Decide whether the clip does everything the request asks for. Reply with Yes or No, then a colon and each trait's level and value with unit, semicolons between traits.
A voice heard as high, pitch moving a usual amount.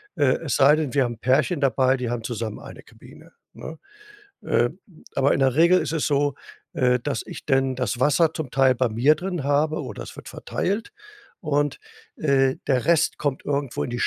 No: low, 135 Hz; average, 3.0 semitones